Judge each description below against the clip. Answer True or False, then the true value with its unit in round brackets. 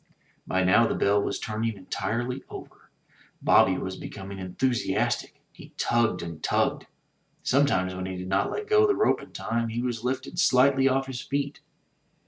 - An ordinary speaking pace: True (170 wpm)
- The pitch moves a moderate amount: False (5.8 semitones)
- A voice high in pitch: False (115 Hz)